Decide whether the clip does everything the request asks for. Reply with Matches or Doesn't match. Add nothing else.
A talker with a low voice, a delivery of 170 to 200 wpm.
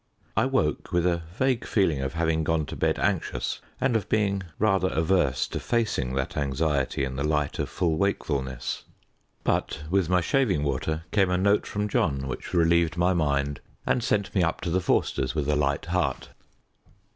Matches